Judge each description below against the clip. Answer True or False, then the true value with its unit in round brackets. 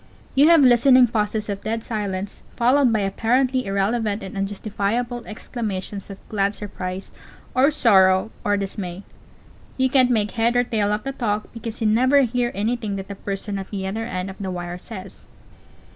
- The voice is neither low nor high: False (215 Hz)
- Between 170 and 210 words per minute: True (175 wpm)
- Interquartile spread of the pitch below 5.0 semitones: True (3.5 semitones)